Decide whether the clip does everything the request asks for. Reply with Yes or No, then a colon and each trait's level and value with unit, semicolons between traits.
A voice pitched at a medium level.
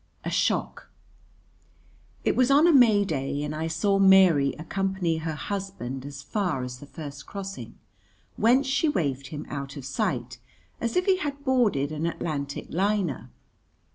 Yes: medium, 165 Hz